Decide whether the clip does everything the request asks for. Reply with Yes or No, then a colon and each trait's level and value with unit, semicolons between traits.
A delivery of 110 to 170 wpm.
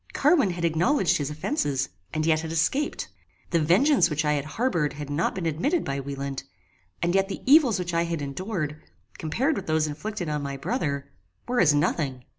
No: average, 190 wpm